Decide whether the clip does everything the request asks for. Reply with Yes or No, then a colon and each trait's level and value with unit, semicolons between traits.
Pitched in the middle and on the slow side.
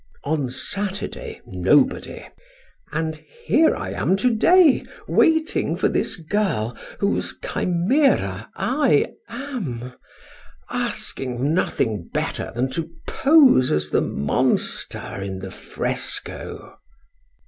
Yes: medium, 160 Hz; slow, 100 wpm